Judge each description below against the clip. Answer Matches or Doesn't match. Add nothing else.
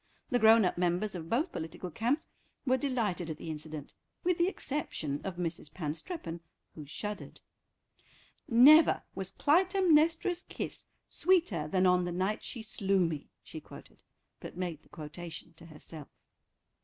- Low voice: Doesn't match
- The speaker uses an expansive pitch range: Matches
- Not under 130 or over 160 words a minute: Matches